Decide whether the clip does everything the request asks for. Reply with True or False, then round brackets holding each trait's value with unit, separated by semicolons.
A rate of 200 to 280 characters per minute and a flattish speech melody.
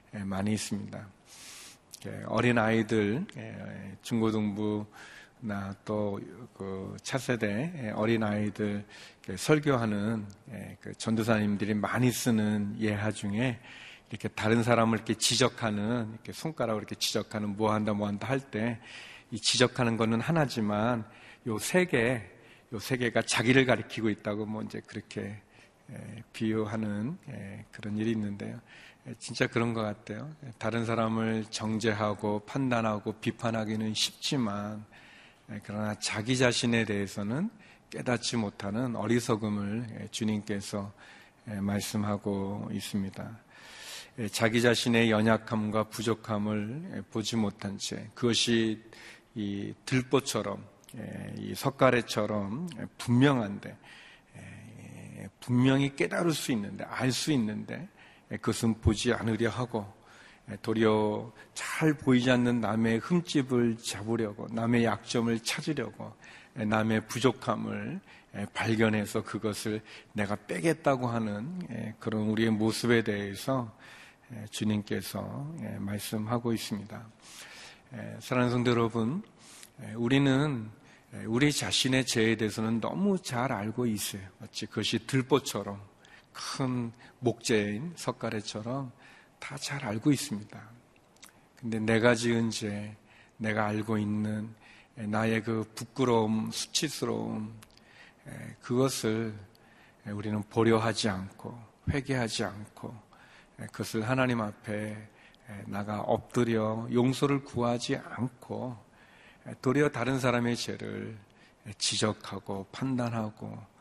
True (245 characters per minute; 2.3 semitones)